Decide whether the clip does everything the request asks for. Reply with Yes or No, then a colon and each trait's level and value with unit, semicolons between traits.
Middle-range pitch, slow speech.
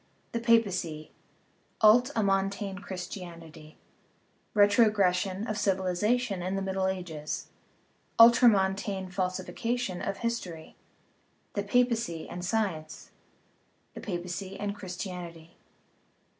No: high, 195 Hz; slow, 100 wpm